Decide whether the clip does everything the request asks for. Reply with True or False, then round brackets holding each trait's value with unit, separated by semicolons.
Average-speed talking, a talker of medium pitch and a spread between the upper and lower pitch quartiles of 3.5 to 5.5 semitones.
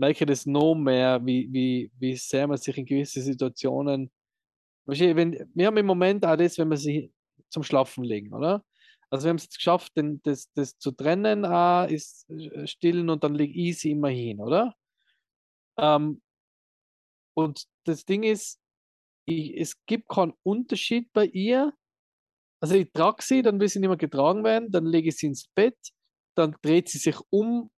True (170 wpm; 160 Hz; 5.2 semitones)